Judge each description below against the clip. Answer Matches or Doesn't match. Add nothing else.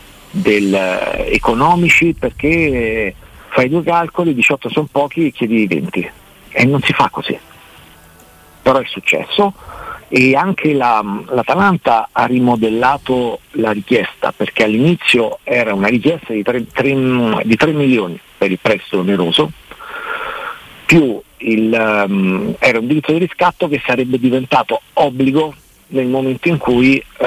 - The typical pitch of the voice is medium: Doesn't match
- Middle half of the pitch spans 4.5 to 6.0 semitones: Matches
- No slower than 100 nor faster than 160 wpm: Matches